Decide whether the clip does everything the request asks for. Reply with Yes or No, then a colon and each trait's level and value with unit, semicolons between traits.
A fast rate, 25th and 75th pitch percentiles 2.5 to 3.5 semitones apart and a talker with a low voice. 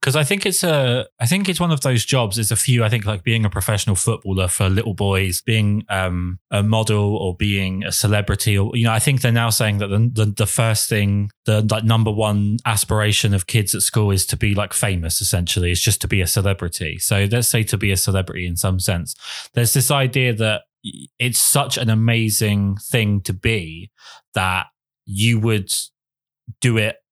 Yes: fast, 210 wpm; average, 2.9 semitones; low, 110 Hz